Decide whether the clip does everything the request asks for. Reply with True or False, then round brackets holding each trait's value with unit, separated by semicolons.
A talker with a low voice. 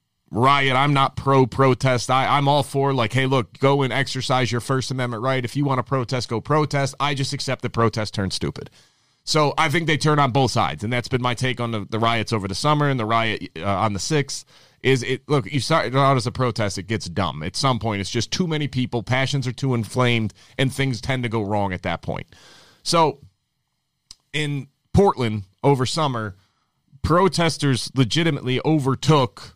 True (130 Hz)